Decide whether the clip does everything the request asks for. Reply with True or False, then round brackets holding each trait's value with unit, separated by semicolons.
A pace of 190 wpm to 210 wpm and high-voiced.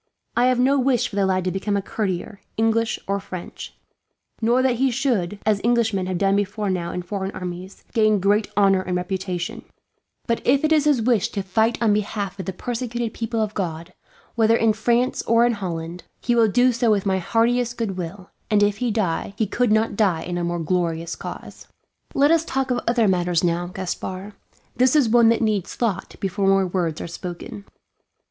True (200 wpm; 205 Hz)